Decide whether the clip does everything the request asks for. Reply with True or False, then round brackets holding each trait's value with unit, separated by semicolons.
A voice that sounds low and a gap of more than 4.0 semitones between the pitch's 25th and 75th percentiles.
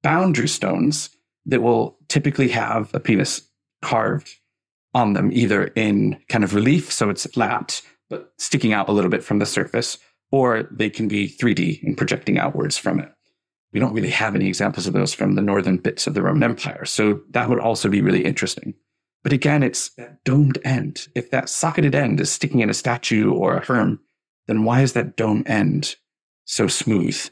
True (120 Hz; 4.4 semitones)